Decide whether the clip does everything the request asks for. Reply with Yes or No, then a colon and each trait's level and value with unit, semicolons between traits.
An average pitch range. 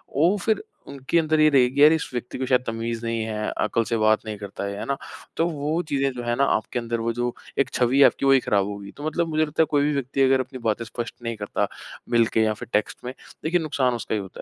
Yes: average, 3.9 semitones